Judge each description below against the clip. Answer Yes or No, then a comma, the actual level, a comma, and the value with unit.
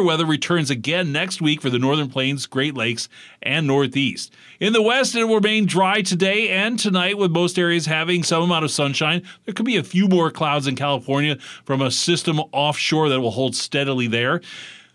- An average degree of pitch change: Yes, average, 4.8 semitones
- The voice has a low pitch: No, medium, 160 Hz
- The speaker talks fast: No, average, 195 wpm